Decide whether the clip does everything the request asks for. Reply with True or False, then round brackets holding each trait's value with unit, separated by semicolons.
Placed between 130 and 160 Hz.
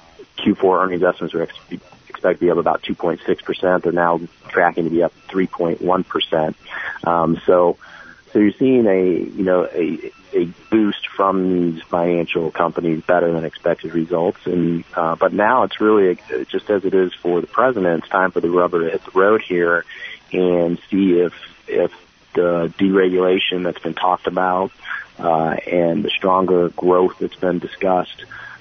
False (90 Hz)